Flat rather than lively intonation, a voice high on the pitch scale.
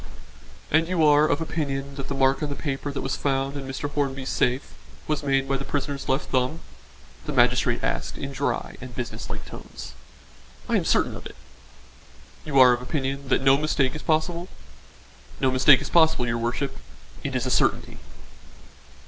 No: narrow, 1.9 semitones; medium, 140 Hz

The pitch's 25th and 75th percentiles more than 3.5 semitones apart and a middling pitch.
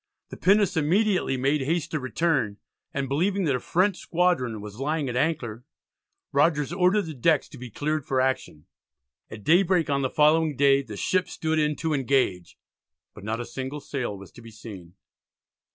Yes: average, 4.7 semitones; medium, 145 Hz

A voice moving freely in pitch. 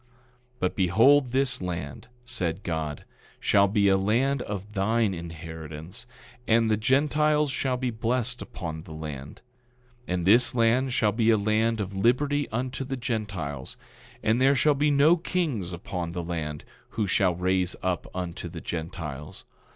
Yes: wide, 6.4 semitones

